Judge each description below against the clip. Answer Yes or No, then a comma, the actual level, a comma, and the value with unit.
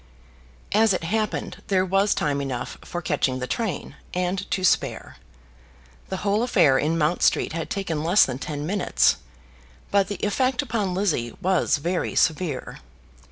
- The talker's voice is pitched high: No, medium, 180 Hz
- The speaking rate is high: No, average, 155 wpm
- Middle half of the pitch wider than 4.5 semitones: Yes, average, 5.0 semitones